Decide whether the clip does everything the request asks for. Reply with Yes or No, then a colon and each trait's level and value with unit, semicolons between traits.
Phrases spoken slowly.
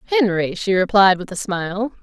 No: average, 175 wpm